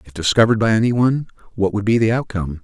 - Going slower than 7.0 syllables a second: No, 7.6 syllables/s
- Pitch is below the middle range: Yes, low, 110 Hz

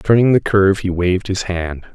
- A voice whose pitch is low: Yes, very low, 95 Hz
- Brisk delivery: Yes, fast, 215 wpm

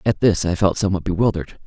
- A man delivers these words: Yes, male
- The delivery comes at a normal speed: No, fast, 215 wpm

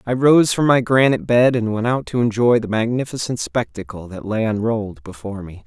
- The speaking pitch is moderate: No, low, 115 Hz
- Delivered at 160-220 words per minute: Yes, average, 200 wpm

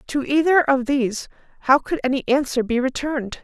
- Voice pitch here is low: No, very high, 270 Hz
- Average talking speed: Yes, average, 175 wpm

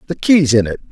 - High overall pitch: No, medium, 140 Hz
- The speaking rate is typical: No, fast, 265 wpm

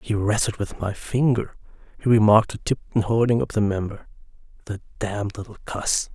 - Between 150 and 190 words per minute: Yes, average, 165 wpm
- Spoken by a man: Yes, male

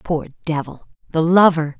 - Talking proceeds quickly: No, slow, 100 wpm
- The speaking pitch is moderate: Yes, medium, 160 Hz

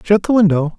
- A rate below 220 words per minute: No, fast, 230 wpm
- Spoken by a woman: No, male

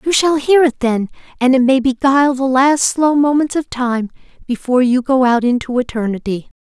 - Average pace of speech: Yes, average, 190 wpm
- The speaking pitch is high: Yes, very high, 260 Hz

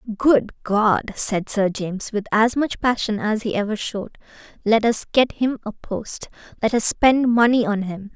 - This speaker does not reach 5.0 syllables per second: Yes, 4.5 syllables/s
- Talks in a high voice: Yes, high, 220 Hz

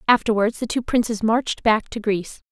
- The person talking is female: Yes, female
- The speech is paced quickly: No, average, 190 wpm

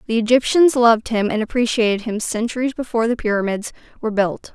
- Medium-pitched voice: No, high, 230 Hz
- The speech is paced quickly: No, average, 170 wpm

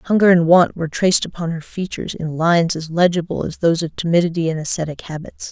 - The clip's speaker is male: No, female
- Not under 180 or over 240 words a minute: Yes, fast, 205 wpm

